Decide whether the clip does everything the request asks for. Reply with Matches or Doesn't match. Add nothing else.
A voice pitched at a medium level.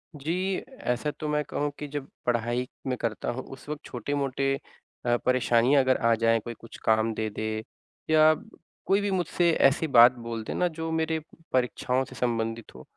Doesn't match